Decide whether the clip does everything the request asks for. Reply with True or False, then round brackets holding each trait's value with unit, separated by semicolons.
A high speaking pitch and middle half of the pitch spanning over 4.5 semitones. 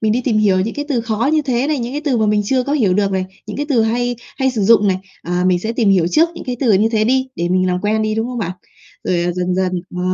True (220 Hz; 5.1 semitones)